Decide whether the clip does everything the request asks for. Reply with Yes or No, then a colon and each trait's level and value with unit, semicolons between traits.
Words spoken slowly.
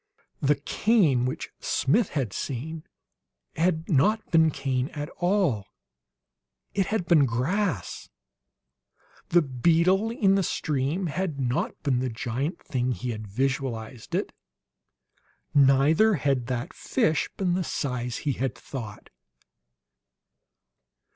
Yes: slow, 115 wpm